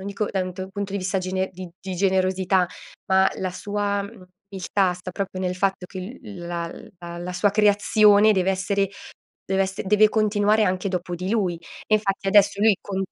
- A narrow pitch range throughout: Yes, narrow, 1.8 semitones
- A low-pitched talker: No, high, 195 Hz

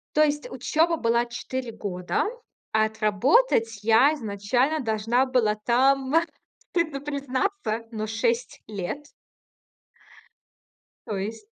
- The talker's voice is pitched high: Yes, high, 240 Hz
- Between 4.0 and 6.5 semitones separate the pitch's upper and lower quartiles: Yes, average, 4.6 semitones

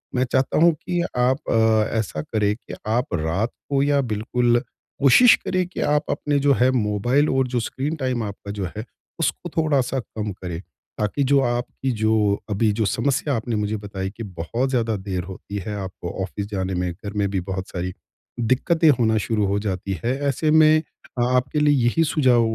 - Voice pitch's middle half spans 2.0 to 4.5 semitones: No, average, 5.0 semitones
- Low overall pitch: Yes, low, 115 Hz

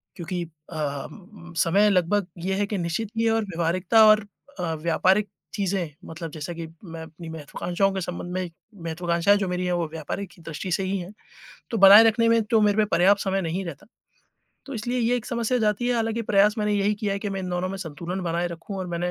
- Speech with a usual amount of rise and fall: Yes, average, 3.6 semitones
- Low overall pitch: No, high, 190 Hz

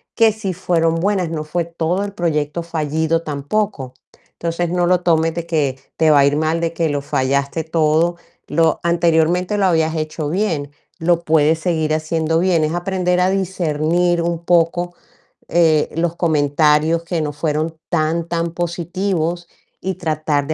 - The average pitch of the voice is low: No, medium, 165 Hz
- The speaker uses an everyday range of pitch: No, narrow, 2.0 semitones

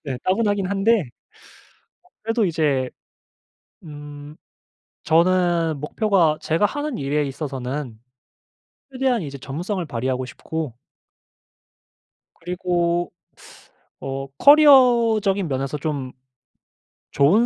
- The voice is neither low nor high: Yes, medium, 165 Hz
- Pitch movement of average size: No, wide, 6.5 semitones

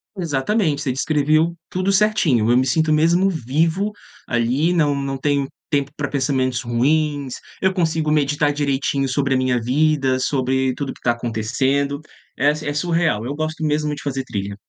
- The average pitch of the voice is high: No, medium, 145 Hz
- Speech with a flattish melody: No, average, 3.1 semitones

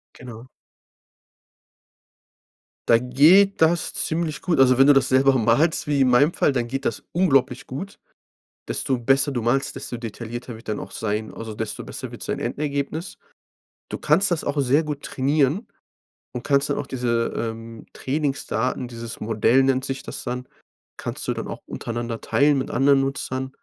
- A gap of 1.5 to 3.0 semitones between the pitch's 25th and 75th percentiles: No, average, 3.4 semitones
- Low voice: Yes, low, 130 Hz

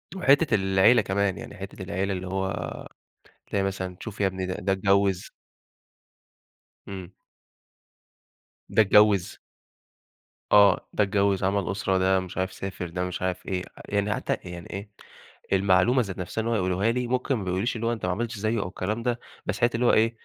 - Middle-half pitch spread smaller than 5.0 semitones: Yes, average, 2.8 semitones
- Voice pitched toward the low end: Yes, low, 100 Hz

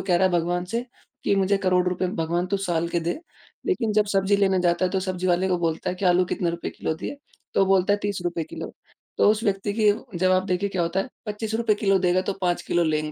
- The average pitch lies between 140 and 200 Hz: Yes, medium, 185 Hz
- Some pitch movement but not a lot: No, narrow, 2.3 semitones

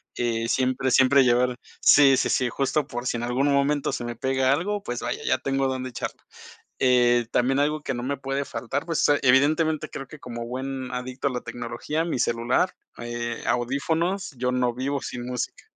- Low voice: Yes, low, 130 Hz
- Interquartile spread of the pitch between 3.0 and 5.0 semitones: No, narrow, 2.5 semitones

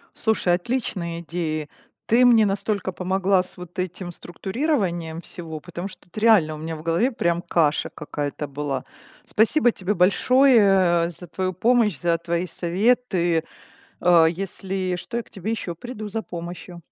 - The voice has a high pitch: No, medium, 180 Hz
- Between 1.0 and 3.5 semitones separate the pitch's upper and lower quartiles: No, average, 4.0 semitones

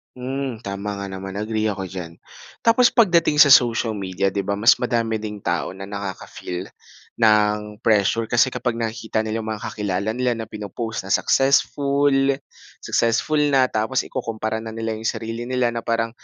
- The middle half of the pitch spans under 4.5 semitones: Yes, average, 3.3 semitones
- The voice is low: Yes, low, 110 Hz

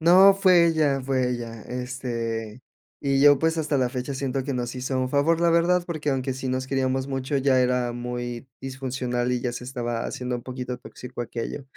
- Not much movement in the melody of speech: Yes, narrow, 2.3 semitones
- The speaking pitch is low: Yes, low, 130 Hz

